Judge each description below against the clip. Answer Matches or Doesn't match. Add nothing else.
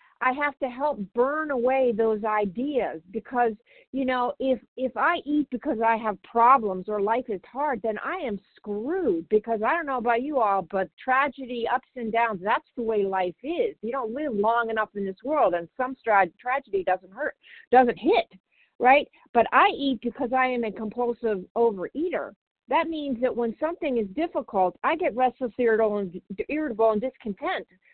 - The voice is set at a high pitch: Matches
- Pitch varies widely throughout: Doesn't match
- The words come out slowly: Doesn't match